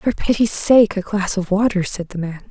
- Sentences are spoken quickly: Yes, fast, 240 wpm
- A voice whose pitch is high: Yes, high, 200 Hz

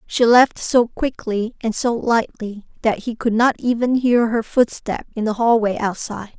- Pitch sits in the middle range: No, high, 230 Hz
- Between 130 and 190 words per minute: Yes, average, 180 wpm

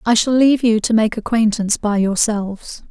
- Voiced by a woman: Yes, female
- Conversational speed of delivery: Yes, average, 185 wpm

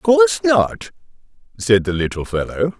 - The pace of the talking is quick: No, slow, 130 wpm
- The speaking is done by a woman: No, male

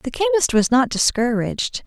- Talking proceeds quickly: No, average, 160 wpm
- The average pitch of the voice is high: Yes, very high, 270 Hz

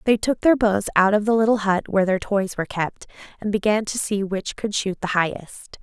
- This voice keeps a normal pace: No, fast, 235 wpm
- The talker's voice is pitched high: Yes, high, 205 Hz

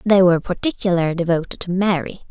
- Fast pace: No, average, 155 wpm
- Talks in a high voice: No, medium, 180 Hz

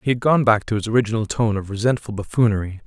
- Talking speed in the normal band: No, fast, 230 wpm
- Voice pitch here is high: No, low, 110 Hz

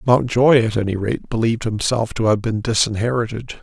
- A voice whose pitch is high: No, low, 115 Hz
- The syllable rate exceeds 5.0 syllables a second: Yes, 5.6 syllables/s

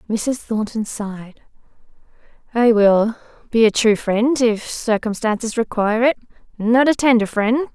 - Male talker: No, female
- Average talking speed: No, slow, 130 wpm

